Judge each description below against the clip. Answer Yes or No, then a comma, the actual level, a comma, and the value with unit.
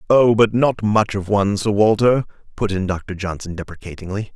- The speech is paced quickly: No, average, 180 wpm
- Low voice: Yes, low, 105 Hz